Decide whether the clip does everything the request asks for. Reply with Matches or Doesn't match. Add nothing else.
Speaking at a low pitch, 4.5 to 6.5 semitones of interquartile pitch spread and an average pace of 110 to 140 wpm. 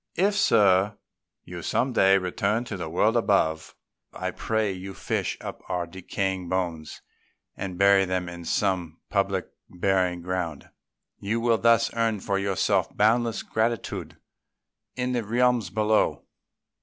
Doesn't match